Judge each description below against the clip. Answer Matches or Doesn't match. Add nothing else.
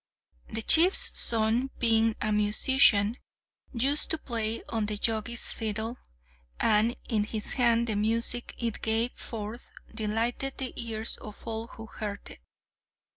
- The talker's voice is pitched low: Doesn't match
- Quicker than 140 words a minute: Doesn't match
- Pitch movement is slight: Matches